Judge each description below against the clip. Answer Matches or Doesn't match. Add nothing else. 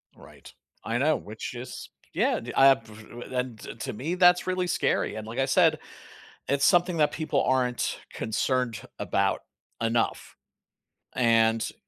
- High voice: Doesn't match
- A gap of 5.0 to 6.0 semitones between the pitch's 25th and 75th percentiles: Matches